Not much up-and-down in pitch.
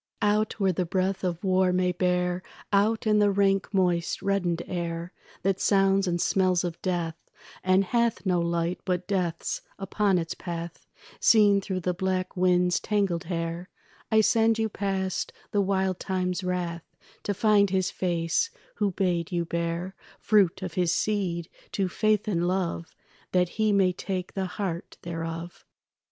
Yes: narrow, 2.2 semitones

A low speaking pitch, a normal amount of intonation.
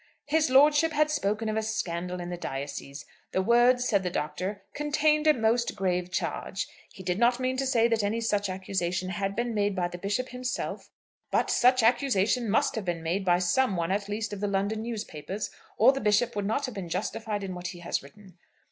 No: high, 205 Hz; average, 4.7 semitones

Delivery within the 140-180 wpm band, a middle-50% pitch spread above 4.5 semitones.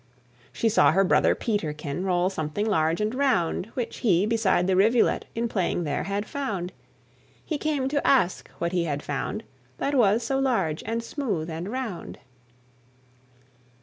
Yes: average, 155 wpm; wide, 5.4 semitones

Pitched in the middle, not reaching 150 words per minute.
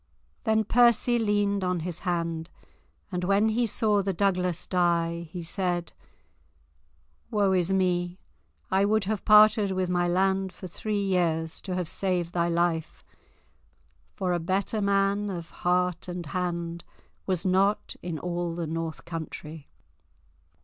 Yes: medium, 180 Hz; average, 140 wpm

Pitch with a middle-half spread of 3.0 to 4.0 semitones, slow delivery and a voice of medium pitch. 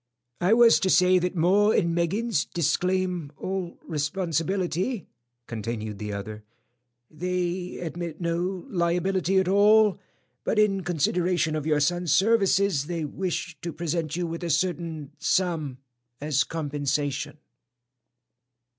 Yes: average, 3.3 semitones; slow, 120 wpm; medium, 175 Hz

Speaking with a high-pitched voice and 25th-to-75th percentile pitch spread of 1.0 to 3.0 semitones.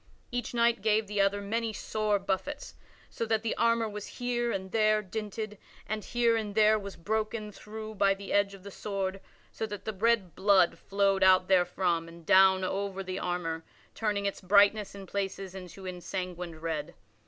Yes: high, 200 Hz; narrow, 2.4 semitones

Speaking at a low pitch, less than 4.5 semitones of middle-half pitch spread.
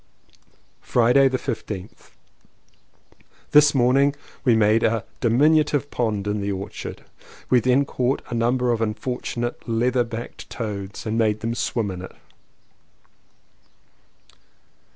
Yes: low, 120 Hz; average, 2.9 semitones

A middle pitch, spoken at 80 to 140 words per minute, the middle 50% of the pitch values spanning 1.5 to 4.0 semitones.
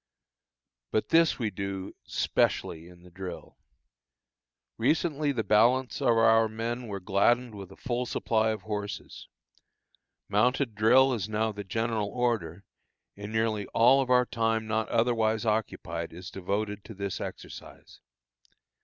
No: low, 110 Hz; slow, 135 wpm; average, 3.0 semitones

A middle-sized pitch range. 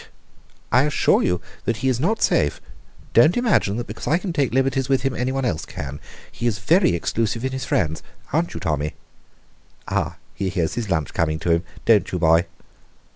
No: wide, 7.8 semitones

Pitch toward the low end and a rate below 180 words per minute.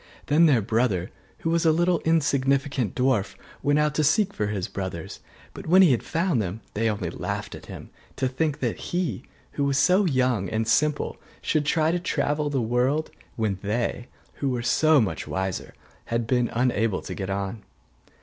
No: low, 130 Hz; average, 190 wpm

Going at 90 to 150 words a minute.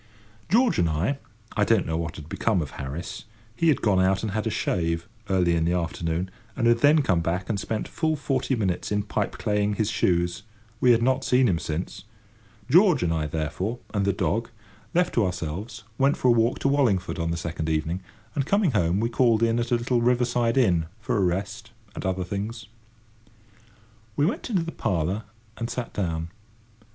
No: average, 195 wpm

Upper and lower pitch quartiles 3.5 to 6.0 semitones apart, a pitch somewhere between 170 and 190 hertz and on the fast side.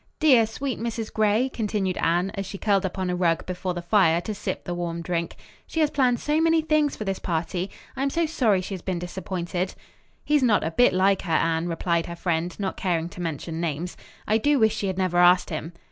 Yes: average, 4.4 semitones; medium, 185 Hz; fast, 230 wpm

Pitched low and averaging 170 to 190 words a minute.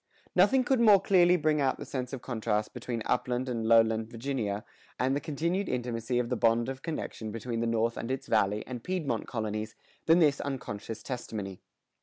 Yes: low, 125 Hz; average, 185 wpm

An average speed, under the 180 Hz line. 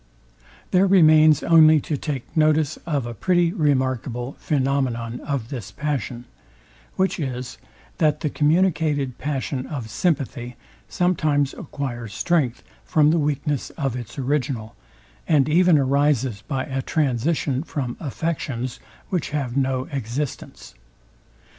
No: slow, 120 wpm; medium, 140 Hz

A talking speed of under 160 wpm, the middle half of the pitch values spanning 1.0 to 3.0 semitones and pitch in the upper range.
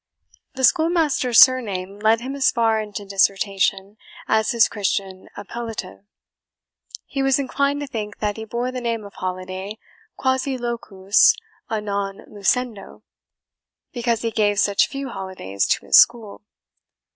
No: slow, 135 wpm; average, 4.1 semitones; high, 220 Hz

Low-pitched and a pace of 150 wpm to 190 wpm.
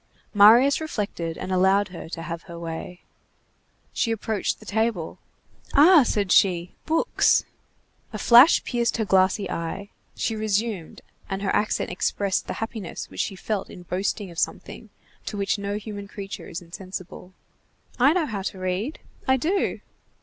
No: high, 200 Hz; average, 155 wpm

